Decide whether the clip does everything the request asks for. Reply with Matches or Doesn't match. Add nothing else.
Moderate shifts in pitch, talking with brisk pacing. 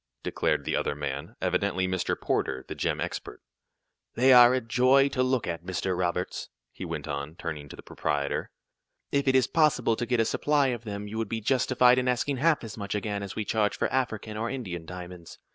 Doesn't match